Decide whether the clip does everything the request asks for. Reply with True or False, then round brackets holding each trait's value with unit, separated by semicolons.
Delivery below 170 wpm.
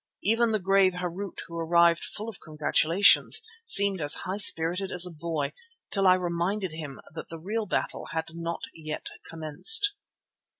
True (160 wpm)